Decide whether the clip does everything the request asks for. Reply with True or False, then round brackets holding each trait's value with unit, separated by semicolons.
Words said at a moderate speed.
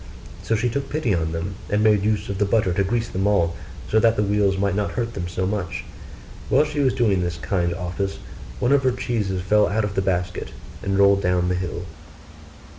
False (220 wpm)